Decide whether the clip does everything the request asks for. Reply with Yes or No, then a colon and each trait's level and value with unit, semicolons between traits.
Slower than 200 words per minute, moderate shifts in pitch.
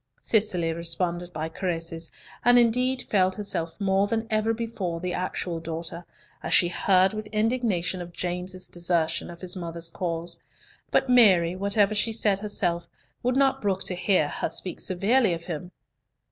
Yes: average, 160 wpm; average, 3.9 semitones